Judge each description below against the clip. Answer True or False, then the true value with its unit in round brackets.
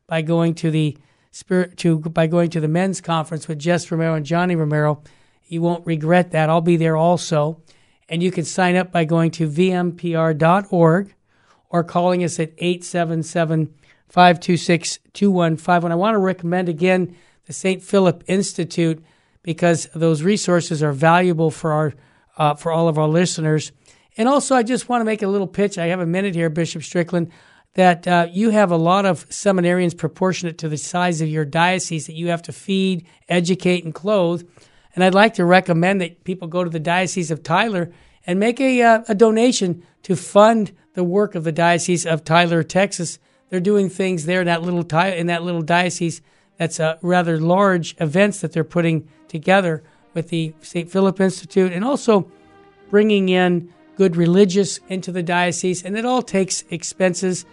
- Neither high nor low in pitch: True (175 Hz)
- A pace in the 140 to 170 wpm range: False (180 wpm)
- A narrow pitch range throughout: True (2.2 semitones)